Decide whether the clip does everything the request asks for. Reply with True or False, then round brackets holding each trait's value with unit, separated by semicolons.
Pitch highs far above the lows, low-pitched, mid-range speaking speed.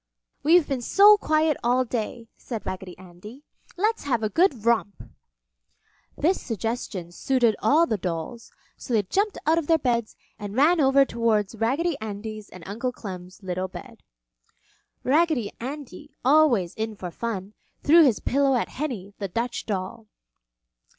False (5.9 semitones; 235 Hz; 150 wpm)